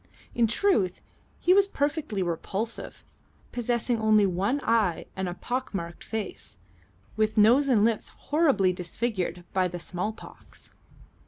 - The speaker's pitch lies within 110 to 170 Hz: No, high, 215 Hz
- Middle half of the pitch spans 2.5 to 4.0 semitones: No, average, 4.9 semitones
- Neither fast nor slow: No, slow, 130 wpm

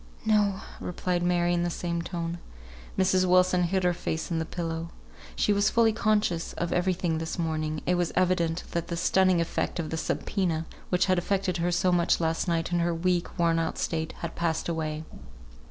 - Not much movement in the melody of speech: Yes, narrow, 1.7 semitones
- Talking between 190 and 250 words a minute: Yes, average, 195 wpm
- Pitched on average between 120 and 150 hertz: No, medium, 175 Hz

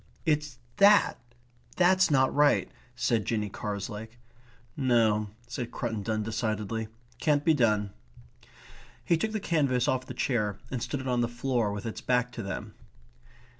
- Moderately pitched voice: No, low, 120 Hz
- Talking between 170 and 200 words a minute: No, average, 145 wpm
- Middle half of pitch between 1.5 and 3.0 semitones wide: No, average, 4.7 semitones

